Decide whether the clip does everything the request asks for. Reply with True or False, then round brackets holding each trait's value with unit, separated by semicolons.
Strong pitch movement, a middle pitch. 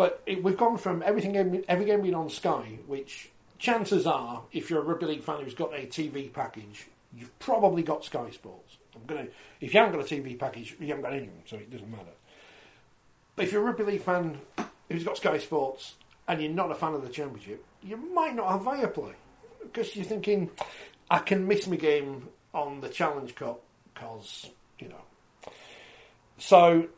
True (6.0 semitones; 170 Hz)